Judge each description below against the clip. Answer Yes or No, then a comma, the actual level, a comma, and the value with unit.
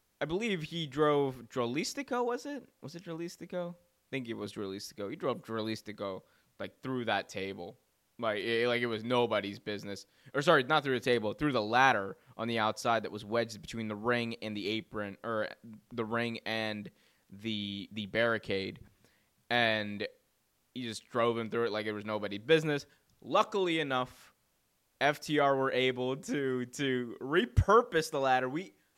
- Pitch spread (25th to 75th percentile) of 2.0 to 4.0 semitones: No, average, 4.7 semitones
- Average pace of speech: Yes, average, 165 wpm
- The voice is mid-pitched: No, low, 120 Hz